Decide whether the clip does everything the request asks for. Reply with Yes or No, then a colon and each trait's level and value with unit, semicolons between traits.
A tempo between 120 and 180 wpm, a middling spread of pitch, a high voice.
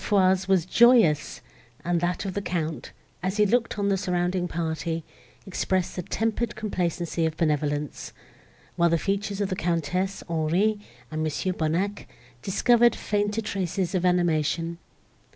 No: average, 140 wpm; average, 3.5 semitones; medium, 180 Hz